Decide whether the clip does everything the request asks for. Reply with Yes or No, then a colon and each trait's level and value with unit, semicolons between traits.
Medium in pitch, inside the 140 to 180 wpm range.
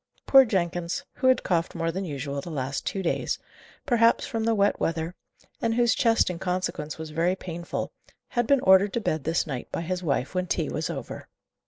No: medium, 180 Hz; average, 200 wpm